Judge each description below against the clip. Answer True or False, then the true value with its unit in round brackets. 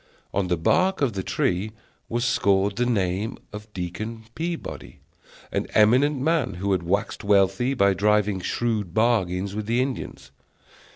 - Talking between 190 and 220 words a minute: False (150 wpm)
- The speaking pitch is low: True (105 Hz)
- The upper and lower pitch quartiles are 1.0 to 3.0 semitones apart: False (3.7 semitones)